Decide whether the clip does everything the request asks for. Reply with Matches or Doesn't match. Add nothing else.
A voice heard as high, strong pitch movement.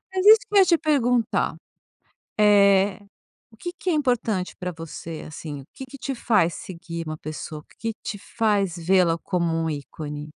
Matches